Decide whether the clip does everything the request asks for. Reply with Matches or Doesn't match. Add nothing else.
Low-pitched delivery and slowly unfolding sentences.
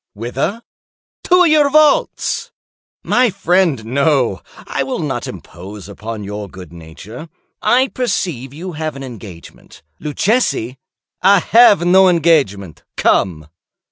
Doesn't match